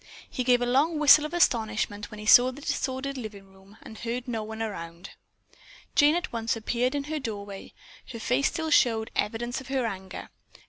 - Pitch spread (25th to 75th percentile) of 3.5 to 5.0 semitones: Yes, average, 4.0 semitones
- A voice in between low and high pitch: No, high, 240 Hz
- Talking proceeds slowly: No, average, 190 wpm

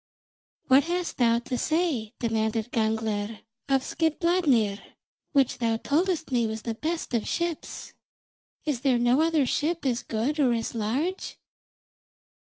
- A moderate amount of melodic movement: No, wide, 5.8 semitones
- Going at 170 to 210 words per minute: No, average, 140 wpm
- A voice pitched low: No, very high, 250 Hz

